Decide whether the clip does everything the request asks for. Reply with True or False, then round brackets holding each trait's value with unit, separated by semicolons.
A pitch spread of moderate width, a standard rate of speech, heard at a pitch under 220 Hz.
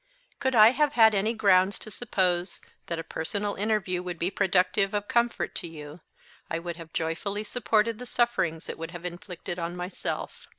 True (3.9 semitones; 180 wpm; 190 Hz)